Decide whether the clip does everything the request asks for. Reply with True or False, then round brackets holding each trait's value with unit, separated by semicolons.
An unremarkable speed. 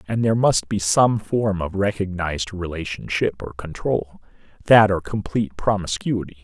False (130 wpm)